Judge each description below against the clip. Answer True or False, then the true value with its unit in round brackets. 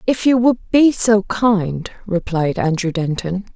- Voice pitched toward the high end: True (200 Hz)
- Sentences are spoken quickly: False (150 wpm)